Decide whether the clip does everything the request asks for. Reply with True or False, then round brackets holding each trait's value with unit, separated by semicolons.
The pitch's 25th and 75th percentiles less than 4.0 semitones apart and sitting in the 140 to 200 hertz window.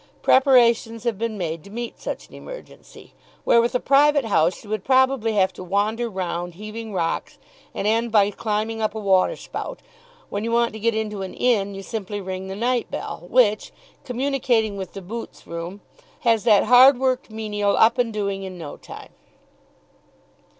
False (3.3 semitones; 220 Hz)